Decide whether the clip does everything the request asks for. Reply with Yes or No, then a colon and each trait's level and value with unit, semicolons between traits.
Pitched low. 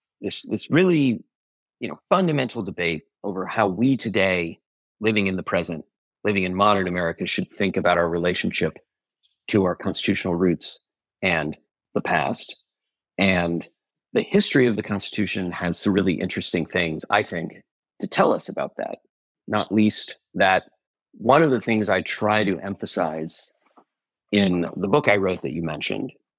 Yes: very low, 95 Hz